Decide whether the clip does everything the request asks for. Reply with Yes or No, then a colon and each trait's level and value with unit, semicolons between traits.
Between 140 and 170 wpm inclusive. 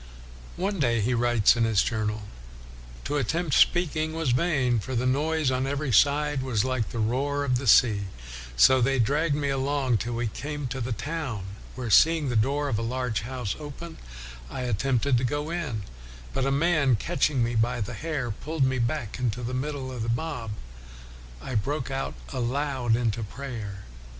No: average, 185 wpm